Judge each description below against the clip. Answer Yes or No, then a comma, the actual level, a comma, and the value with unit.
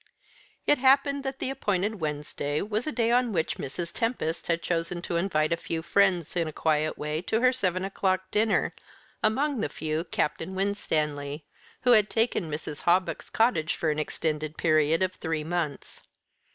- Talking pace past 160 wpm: Yes, average, 170 wpm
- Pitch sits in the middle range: Yes, medium, 175 Hz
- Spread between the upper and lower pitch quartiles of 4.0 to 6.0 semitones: Yes, wide, 5.6 semitones